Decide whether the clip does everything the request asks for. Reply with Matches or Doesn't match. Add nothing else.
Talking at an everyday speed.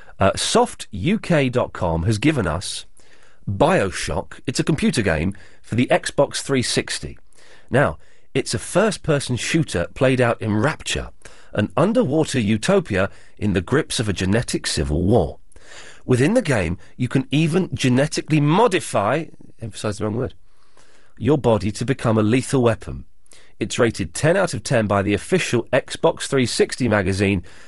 Matches